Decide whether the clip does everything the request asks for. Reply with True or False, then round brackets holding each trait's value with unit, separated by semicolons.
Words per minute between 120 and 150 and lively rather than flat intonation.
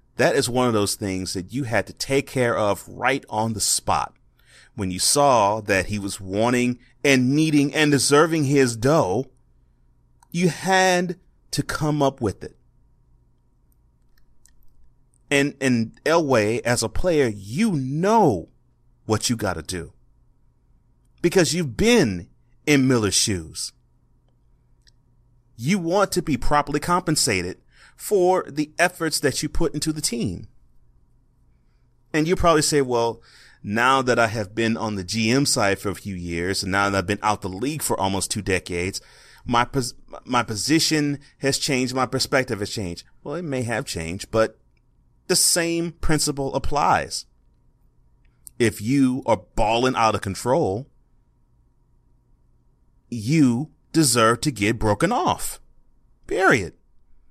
True (140 wpm; 5.8 semitones)